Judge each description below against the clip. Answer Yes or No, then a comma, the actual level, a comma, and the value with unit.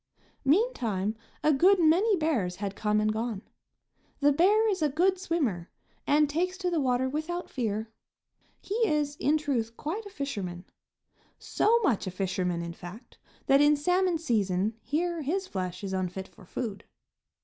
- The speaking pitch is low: No, very high, 280 Hz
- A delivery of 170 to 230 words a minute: No, average, 160 wpm